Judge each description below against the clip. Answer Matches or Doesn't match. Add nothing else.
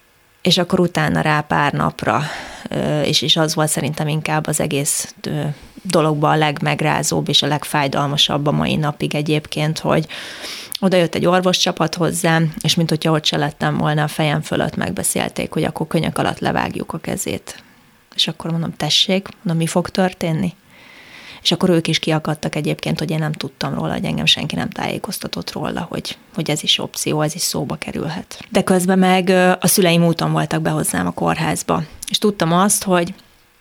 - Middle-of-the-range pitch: Matches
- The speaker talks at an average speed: Doesn't match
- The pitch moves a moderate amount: Matches